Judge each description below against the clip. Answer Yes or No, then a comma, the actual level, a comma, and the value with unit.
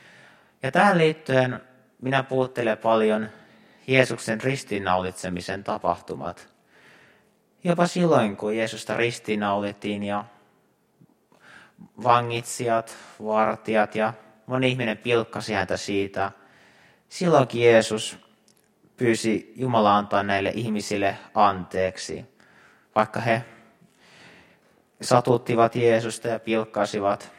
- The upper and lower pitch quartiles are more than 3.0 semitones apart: No, narrow, 2.5 semitones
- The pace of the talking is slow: Yes, slow, 80 wpm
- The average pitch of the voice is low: Yes, low, 110 Hz